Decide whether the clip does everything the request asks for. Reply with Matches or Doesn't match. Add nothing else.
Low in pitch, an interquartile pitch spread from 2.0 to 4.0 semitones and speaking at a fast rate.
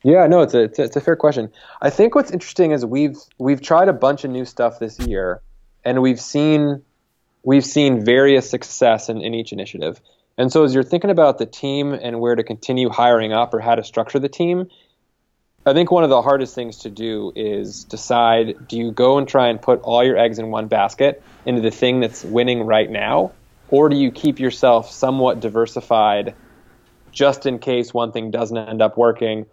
Matches